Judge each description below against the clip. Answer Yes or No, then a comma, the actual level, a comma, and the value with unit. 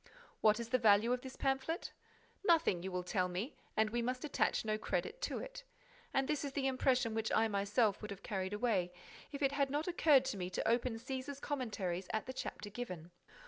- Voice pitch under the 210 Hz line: No, high, 235 Hz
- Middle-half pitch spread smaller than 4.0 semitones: No, average, 4.8 semitones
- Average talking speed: No, fast, 210 wpm